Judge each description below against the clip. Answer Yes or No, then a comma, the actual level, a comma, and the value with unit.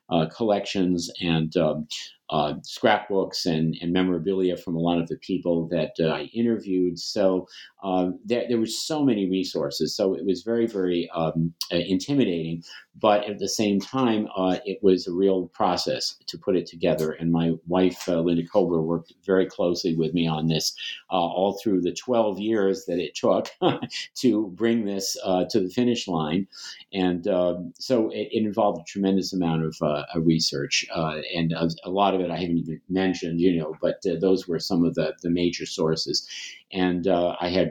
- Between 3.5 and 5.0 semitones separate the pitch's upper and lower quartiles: No, average, 2.9 semitones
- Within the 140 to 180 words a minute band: No, average, 190 wpm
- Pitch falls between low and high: No, very low, 90 Hz